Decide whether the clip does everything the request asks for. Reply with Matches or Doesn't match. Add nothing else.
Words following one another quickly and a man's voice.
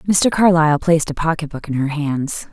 Doesn't match